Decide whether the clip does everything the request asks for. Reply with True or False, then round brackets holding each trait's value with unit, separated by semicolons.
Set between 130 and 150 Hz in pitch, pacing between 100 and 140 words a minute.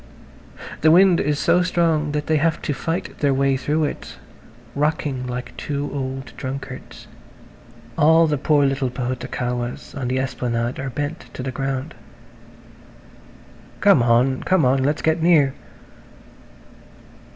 True (140 Hz; 135 wpm)